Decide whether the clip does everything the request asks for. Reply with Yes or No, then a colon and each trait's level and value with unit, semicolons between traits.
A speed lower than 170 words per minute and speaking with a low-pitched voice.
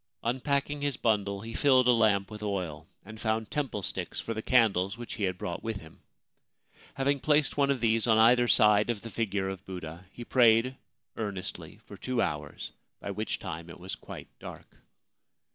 No: average, 185 wpm; low, 110 Hz